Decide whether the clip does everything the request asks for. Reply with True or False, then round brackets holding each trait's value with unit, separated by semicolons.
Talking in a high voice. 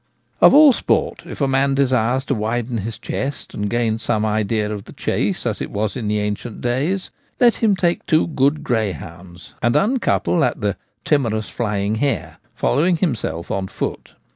False (120 Hz)